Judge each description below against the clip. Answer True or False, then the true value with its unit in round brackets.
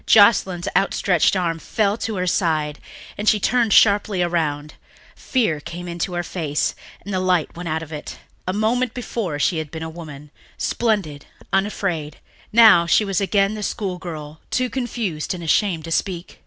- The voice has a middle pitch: True (180 Hz)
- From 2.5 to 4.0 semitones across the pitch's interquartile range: False (4.4 semitones)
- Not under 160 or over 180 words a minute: True (170 wpm)